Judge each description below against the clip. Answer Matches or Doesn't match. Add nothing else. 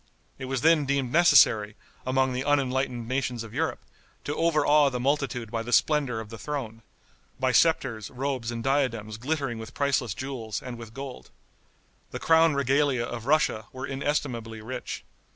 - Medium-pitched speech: Doesn't match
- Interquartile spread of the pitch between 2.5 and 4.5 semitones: Matches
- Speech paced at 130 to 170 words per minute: Matches